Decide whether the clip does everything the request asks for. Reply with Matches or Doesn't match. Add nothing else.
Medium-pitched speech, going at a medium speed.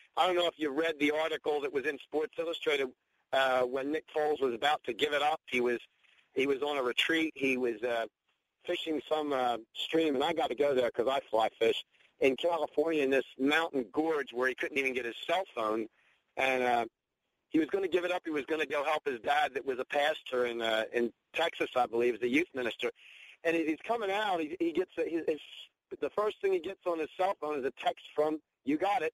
Doesn't match